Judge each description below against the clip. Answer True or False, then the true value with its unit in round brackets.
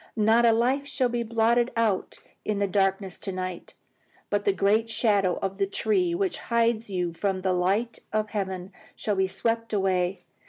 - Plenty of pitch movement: False (3.4 semitones)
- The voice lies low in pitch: False (210 Hz)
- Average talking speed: True (170 wpm)